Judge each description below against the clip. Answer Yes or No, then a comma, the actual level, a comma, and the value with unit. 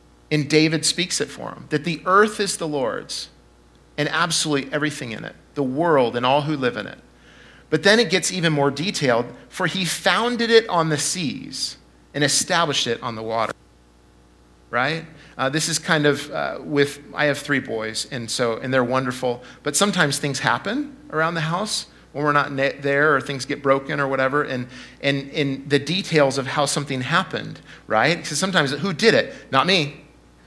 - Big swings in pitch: No, average, 4.7 semitones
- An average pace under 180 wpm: No, average, 190 wpm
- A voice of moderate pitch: Yes, medium, 145 Hz